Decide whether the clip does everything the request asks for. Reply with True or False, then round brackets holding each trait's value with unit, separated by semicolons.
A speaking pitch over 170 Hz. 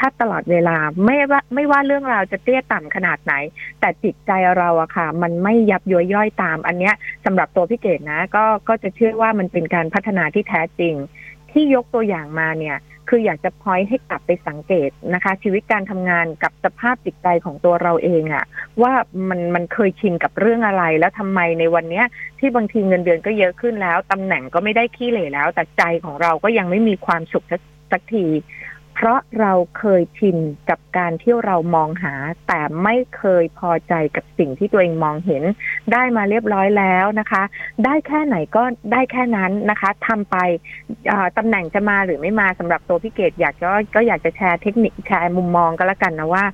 True (185 Hz)